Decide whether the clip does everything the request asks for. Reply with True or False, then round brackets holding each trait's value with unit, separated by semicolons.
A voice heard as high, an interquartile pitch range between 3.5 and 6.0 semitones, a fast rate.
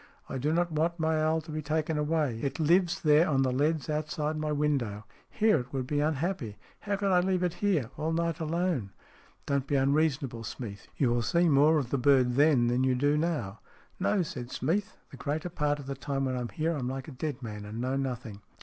False (150 Hz; 3.8 semitones; 240 wpm)